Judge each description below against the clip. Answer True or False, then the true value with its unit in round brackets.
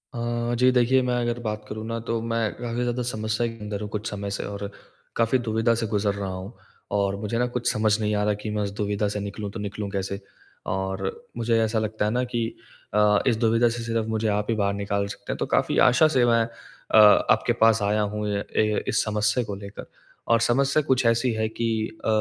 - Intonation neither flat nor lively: False (2.1 semitones)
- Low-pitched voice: True (110 Hz)